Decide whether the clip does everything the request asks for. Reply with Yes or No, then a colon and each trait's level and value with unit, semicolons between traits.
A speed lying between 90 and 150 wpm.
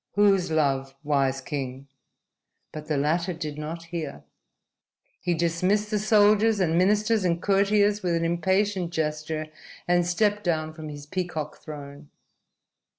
Yes: slow, 135 wpm